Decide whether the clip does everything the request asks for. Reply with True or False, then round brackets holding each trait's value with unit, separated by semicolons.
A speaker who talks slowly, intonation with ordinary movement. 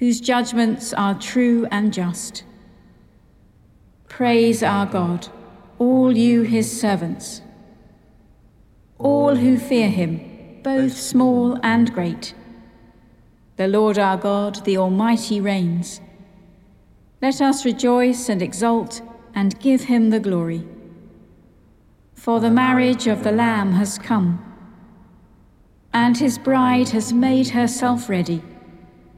True (110 wpm; 4.1 semitones)